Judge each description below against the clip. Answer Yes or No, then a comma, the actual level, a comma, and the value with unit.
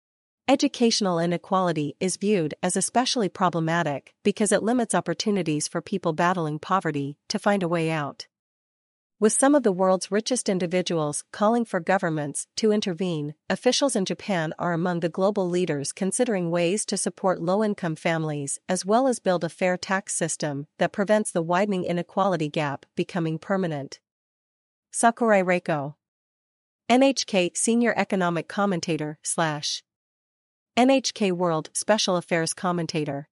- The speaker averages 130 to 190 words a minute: Yes, slow, 135 wpm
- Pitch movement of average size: Yes, average, 3.8 semitones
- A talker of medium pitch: Yes, medium, 180 Hz